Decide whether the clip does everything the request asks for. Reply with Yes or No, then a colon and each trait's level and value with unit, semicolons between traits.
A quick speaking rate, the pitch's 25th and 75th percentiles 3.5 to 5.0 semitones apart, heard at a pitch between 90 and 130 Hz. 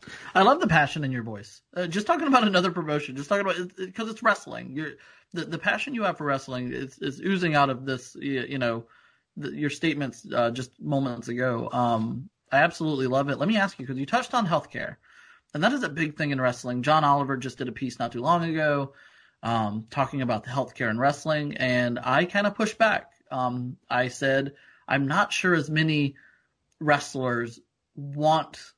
No: fast, 210 wpm; average, 4.6 semitones; medium, 140 Hz